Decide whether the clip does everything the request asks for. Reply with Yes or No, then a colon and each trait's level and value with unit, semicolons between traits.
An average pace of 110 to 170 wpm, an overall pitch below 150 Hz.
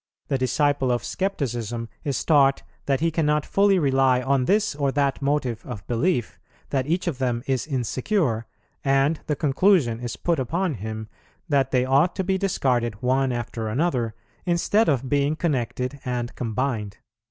Yes: average, 160 wpm; low, 135 Hz